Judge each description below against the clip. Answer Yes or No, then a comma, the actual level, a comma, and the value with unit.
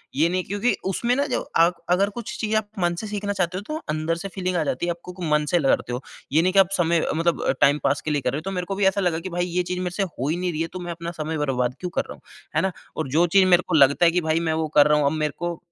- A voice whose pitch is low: No, medium, 175 Hz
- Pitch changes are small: No, average, 3.1 semitones